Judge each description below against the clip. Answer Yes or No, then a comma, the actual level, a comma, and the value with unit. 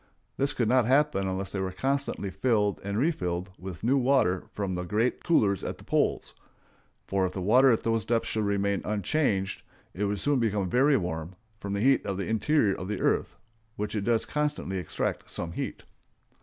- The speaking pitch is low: Yes, low, 105 Hz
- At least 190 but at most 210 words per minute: Yes, average, 195 wpm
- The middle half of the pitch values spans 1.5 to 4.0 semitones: No, average, 4.8 semitones